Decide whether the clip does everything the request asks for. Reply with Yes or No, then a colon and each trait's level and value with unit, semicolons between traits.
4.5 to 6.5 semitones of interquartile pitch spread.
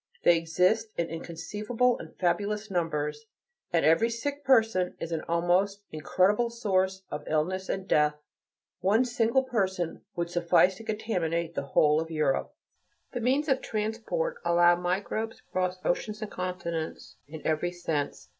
Yes: average, 4.8 semitones